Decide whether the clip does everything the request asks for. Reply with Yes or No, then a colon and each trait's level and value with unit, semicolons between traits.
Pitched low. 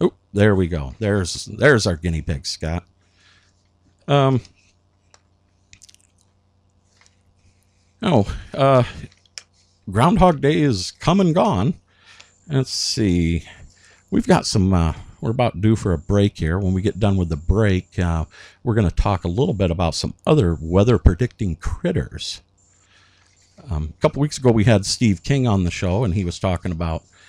Yes: low, 100 Hz